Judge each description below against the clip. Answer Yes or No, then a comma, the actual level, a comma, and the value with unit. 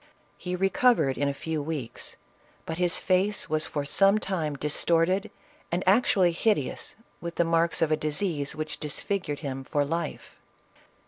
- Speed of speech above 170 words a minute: No, average, 155 wpm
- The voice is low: No, medium, 165 Hz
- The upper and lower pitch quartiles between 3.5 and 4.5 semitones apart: Yes, average, 3.8 semitones